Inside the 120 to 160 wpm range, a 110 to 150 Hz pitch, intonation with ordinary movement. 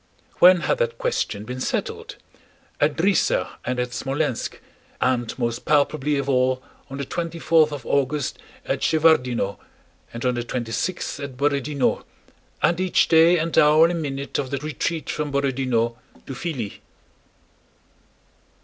Yes: average, 145 wpm; medium, 140 Hz; average, 4.0 semitones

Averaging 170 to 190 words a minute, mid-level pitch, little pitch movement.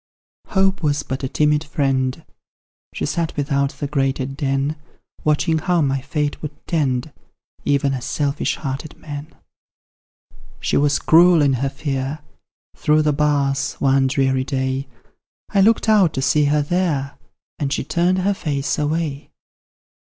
No: average, 145 wpm; medium, 145 Hz; narrow, 2.3 semitones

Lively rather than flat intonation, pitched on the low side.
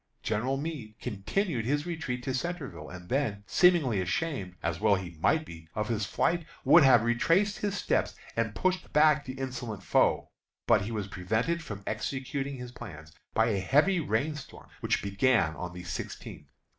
Yes: wide, 7.0 semitones; low, 120 Hz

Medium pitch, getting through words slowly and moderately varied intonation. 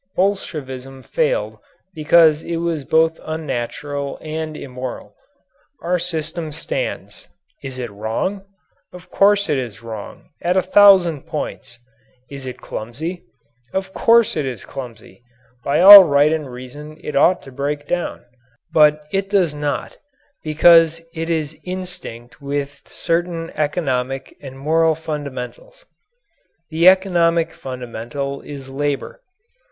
Yes: medium, 155 Hz; slow, 125 wpm; average, 4.4 semitones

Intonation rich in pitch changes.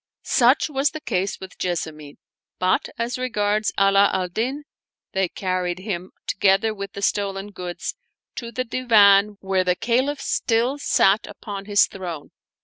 No: average, 3.9 semitones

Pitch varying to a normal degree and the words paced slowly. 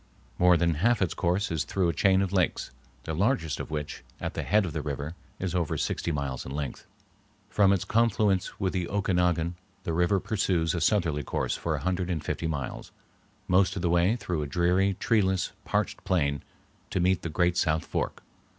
No: average, 3.0 semitones; average, 195 wpm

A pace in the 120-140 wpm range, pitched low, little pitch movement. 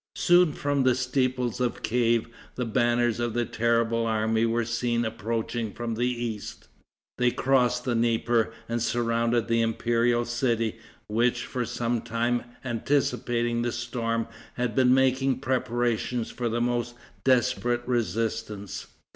Yes: slow, 135 wpm; low, 120 Hz; narrow, 1.2 semitones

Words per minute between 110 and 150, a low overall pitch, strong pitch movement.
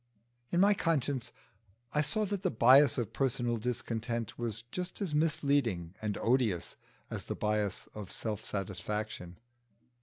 Yes: average, 140 wpm; low, 120 Hz; wide, 5.7 semitones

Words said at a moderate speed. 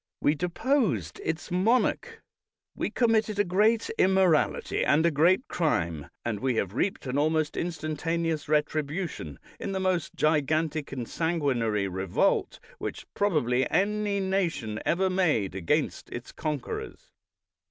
No: slow, 130 wpm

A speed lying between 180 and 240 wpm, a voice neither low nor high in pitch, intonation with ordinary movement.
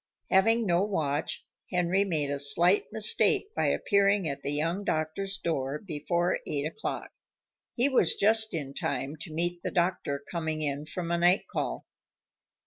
No: average, 155 wpm; medium, 170 Hz; average, 4.7 semitones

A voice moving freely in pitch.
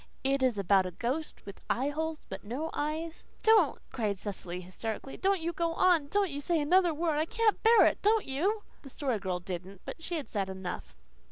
Yes: wide, 8.7 semitones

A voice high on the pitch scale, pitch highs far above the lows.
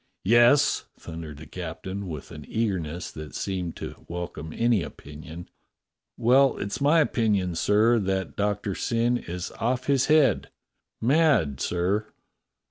No: low, 100 Hz; wide, 5.8 semitones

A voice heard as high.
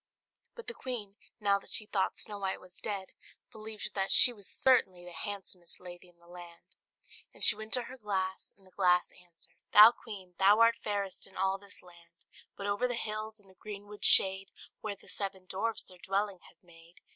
Yes: high, 195 Hz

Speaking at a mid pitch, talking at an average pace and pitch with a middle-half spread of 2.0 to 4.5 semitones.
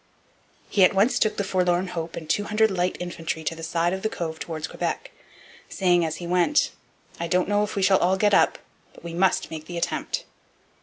No: medium, 180 Hz; fast, 210 wpm; average, 2.9 semitones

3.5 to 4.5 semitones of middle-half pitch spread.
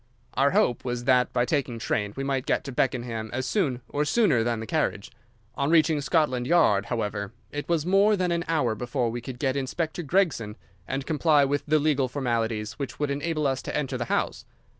Yes: average, 4.1 semitones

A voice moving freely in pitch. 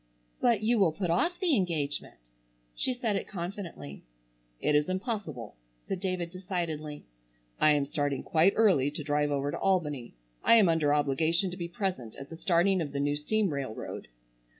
No: average, 4.9 semitones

